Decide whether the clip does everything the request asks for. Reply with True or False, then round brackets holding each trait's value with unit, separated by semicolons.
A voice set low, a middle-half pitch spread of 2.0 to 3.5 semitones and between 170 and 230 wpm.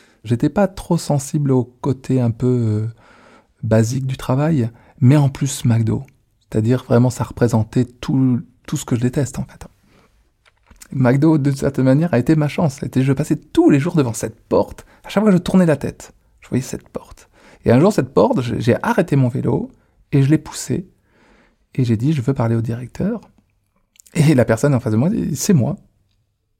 False (130 Hz; 4.2 semitones; 200 wpm)